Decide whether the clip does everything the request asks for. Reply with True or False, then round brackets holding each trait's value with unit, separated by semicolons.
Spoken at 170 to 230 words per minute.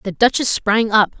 True (200 wpm)